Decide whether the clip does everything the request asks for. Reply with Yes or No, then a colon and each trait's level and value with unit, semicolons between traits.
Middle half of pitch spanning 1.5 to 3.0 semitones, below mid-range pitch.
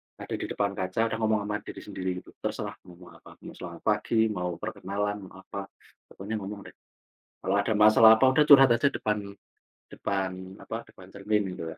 Yes: average, 2.7 semitones; low, 105 Hz